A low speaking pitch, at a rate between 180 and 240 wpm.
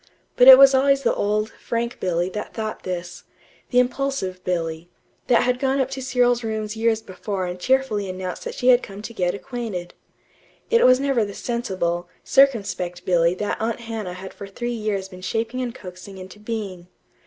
No: high, 215 Hz; average, 185 wpm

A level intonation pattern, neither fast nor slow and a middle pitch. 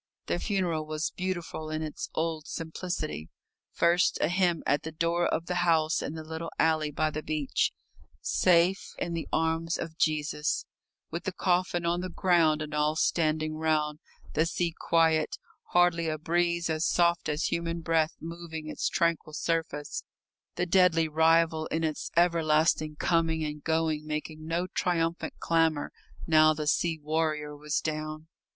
Yes: narrow, 1.6 semitones; average, 155 wpm; medium, 160 Hz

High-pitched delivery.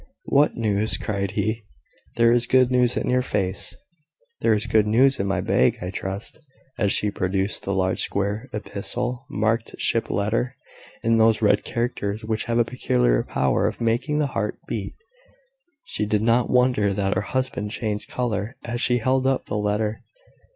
No: low, 110 Hz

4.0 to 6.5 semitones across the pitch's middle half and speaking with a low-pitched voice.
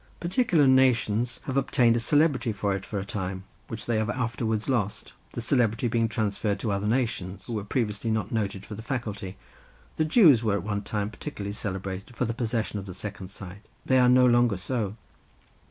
No: average, 3.5 semitones; low, 110 Hz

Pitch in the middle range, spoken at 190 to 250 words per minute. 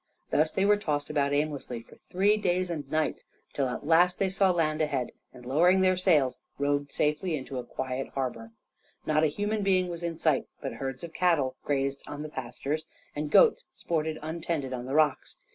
Yes: medium, 155 Hz; average, 195 wpm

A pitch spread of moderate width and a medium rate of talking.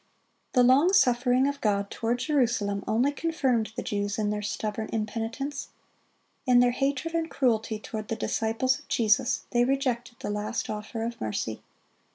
Yes: average, 3.4 semitones; average, 160 wpm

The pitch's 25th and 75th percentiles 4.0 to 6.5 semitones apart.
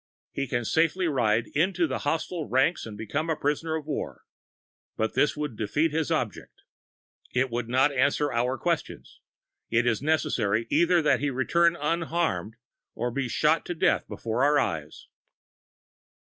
Yes: average, 5.1 semitones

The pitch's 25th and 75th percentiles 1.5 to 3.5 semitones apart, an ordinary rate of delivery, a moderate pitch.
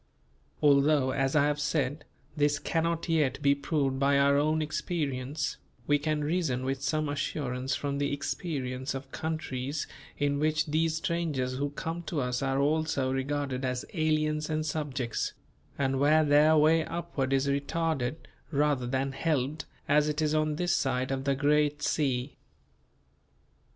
Yes: narrow, 2.4 semitones; average, 150 wpm; medium, 145 Hz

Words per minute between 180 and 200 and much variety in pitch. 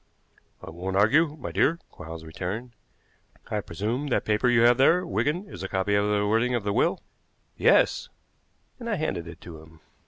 Yes: average, 185 wpm; wide, 6.0 semitones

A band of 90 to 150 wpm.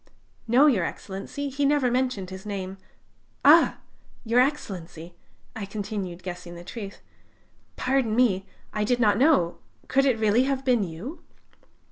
Yes: average, 140 wpm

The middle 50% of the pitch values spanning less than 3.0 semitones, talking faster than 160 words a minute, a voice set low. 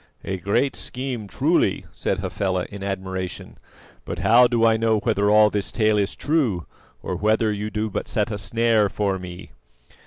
Yes: narrow, 2.5 semitones; average, 175 wpm; low, 105 Hz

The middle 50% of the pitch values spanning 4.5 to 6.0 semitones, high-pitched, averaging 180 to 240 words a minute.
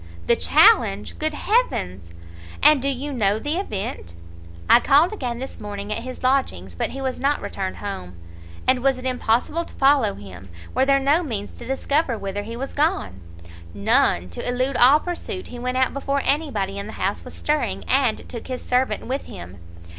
Yes: wide, 5.5 semitones; very high, 255 Hz; average, 190 wpm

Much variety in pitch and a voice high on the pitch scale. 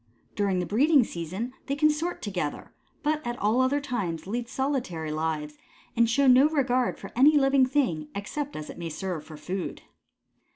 Yes: wide, 8.2 semitones; high, 240 Hz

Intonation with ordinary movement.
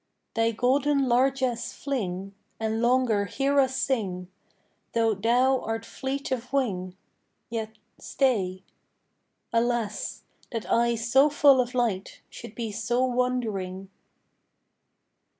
Yes: average, 3.2 semitones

